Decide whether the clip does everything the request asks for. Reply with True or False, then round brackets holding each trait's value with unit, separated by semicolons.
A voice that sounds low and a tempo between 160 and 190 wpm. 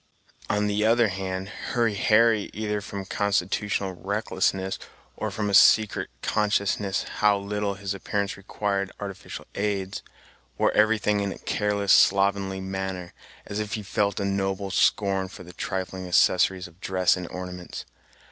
False (100 Hz; 145 wpm)